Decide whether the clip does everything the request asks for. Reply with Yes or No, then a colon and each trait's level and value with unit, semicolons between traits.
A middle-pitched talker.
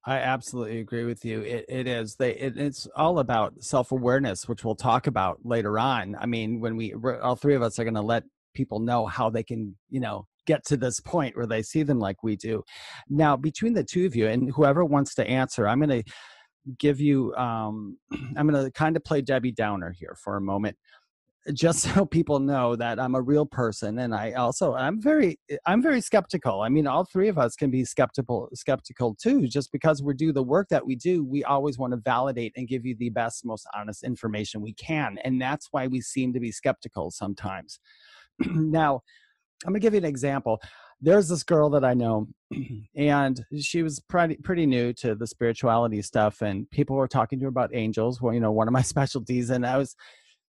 No: low, 130 Hz